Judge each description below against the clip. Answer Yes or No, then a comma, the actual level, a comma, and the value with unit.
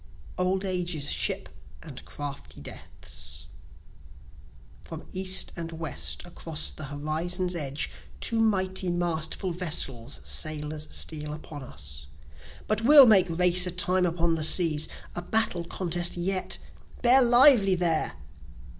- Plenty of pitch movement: No, average, 3.3 semitones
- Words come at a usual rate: No, slow, 120 wpm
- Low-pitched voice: No, medium, 175 Hz